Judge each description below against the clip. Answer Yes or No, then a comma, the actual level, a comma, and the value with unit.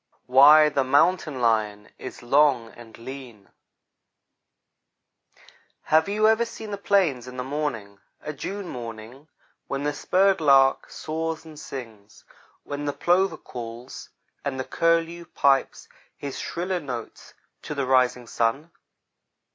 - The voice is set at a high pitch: No, medium, 140 Hz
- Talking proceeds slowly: Yes, slow, 130 wpm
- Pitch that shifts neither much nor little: Yes, average, 4.9 semitones